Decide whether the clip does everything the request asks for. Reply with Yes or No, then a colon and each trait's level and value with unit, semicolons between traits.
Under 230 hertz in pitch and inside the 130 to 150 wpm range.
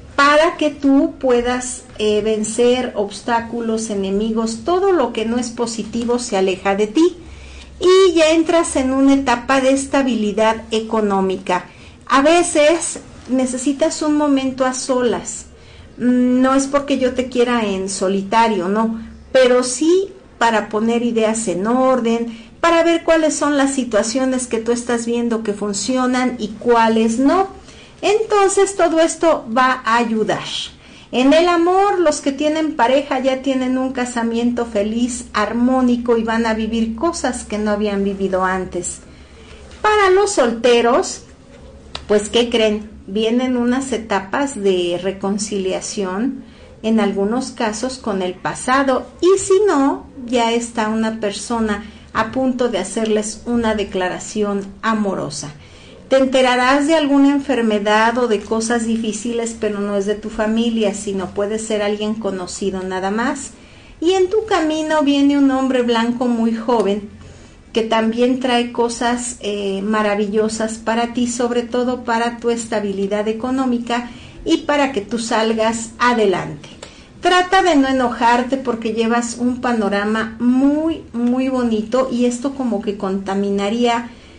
No: high, 235 Hz; average, 135 wpm